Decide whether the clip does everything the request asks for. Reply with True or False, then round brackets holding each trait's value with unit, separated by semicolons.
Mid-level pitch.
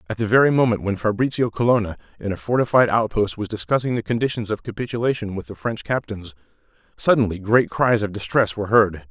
False (110 Hz)